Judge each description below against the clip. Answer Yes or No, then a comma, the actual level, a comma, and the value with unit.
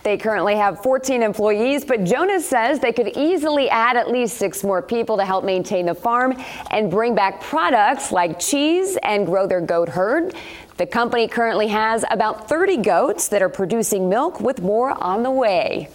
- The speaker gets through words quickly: No, average, 185 wpm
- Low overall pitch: No, high, 225 Hz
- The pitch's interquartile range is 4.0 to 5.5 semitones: Yes, average, 4.8 semitones